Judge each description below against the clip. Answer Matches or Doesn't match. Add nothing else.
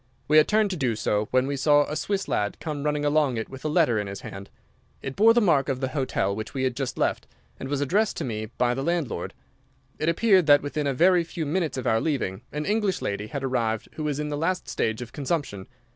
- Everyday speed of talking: Doesn't match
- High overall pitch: Doesn't match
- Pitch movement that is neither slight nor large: Matches